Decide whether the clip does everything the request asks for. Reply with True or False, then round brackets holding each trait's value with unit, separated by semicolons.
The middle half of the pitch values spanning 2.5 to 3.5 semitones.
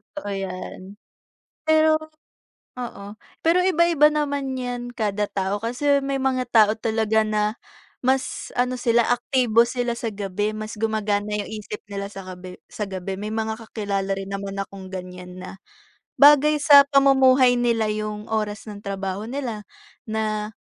False (4.2 semitones)